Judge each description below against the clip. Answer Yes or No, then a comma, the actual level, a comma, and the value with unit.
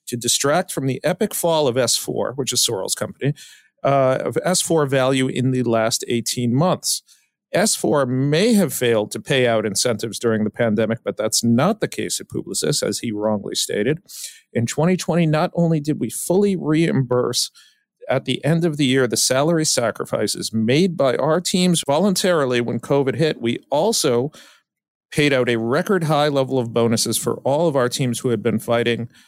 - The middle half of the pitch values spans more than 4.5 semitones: Yes, average, 5.2 semitones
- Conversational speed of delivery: Yes, average, 180 wpm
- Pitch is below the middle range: Yes, low, 130 Hz